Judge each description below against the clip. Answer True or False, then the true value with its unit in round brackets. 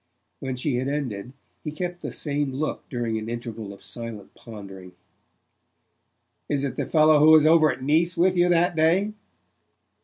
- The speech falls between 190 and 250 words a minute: False (165 wpm)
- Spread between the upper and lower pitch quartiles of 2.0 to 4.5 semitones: False (5.5 semitones)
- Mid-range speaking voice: True (145 Hz)